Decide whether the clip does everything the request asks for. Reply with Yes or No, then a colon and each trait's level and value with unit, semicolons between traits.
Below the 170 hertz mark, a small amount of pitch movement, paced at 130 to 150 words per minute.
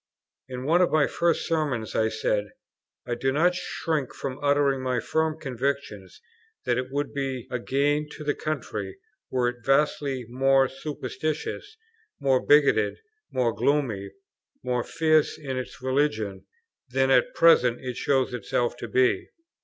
No: low, 135 Hz; average, 3.2 semitones; average, 145 wpm